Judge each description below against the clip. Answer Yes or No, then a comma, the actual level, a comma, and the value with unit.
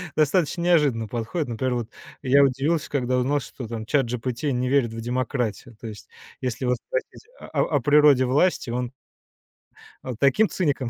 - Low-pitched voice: Yes, low, 130 Hz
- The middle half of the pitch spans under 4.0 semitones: Yes, average, 3.2 semitones